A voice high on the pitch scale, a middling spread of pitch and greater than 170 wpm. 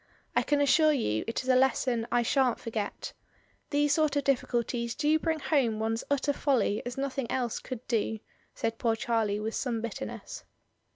Yes: high, 245 Hz; average, 3.8 semitones; average, 180 wpm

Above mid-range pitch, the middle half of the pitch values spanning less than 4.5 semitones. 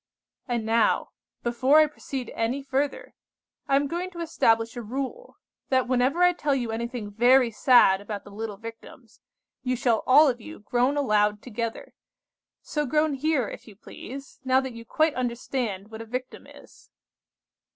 Yes: very high, 250 Hz; average, 3.5 semitones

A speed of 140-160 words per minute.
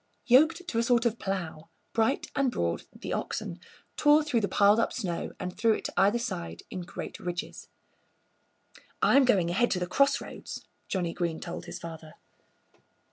No: average, 170 wpm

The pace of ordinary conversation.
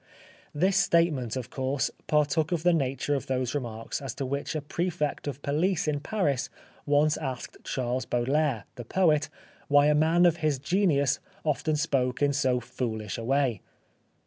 Yes: average, 165 wpm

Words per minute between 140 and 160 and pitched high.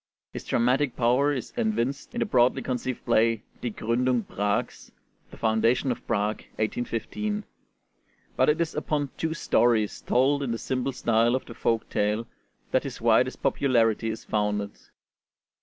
No: average, 150 wpm; low, 120 Hz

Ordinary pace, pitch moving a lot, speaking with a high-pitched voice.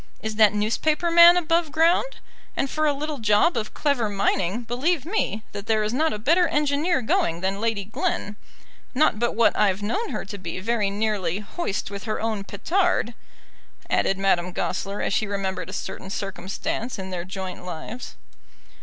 Yes: average, 175 wpm; wide, 7.0 semitones; high, 215 Hz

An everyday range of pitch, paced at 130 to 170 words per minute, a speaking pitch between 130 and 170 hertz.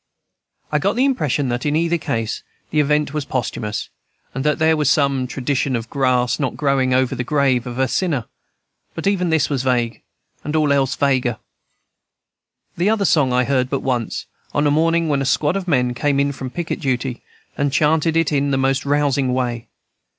No: average, 3.0 semitones; average, 195 wpm; medium, 140 Hz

